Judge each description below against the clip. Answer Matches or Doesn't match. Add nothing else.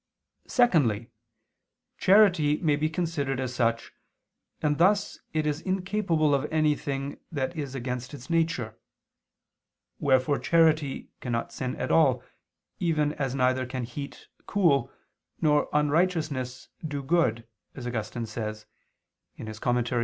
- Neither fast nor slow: Doesn't match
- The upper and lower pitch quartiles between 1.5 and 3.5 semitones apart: Doesn't match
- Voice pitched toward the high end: Doesn't match